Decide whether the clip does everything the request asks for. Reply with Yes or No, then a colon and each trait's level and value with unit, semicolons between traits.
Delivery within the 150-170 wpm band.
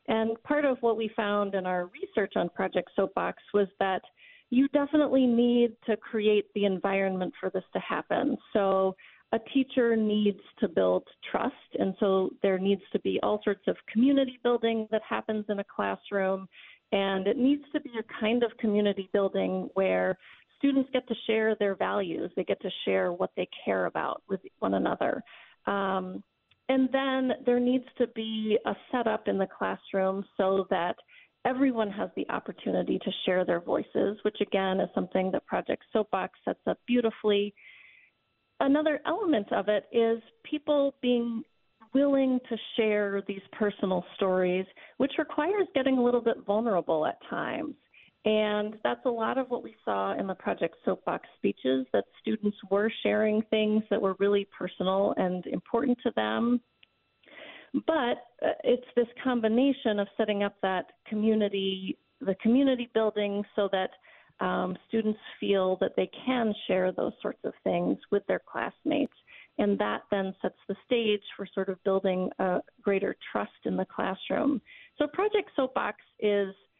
Yes: average, 160 wpm